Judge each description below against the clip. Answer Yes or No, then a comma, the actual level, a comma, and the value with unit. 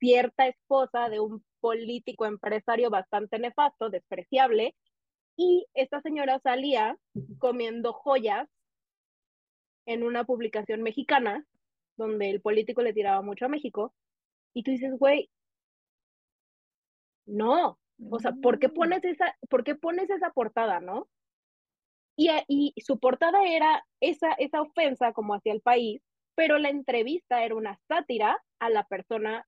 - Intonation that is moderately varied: Yes, average, 4.2 semitones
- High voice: Yes, high, 245 Hz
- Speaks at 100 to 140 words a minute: Yes, average, 130 wpm